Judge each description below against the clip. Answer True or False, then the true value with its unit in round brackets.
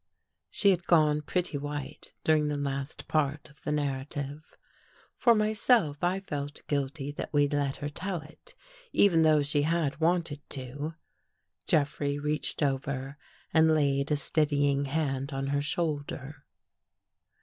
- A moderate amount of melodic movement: False (1.9 semitones)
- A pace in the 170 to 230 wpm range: False (140 wpm)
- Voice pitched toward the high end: False (145 Hz)